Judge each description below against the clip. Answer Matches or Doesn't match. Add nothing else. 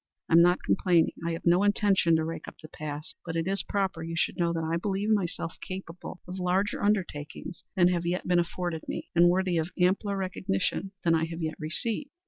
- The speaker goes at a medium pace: Doesn't match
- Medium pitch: Matches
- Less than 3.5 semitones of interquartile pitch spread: Matches